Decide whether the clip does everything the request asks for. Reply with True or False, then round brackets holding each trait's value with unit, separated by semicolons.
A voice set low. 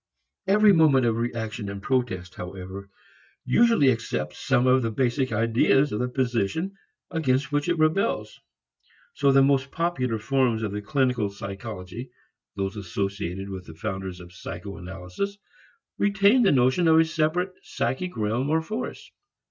True (125 Hz)